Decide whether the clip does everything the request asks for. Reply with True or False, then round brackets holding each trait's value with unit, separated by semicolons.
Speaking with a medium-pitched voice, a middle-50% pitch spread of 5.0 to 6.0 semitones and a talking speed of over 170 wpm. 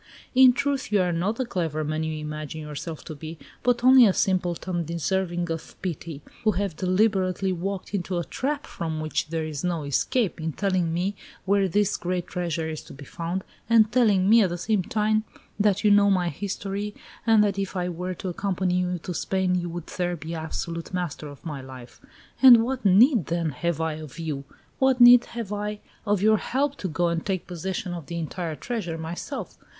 False (180 Hz; 4.0 semitones; 200 wpm)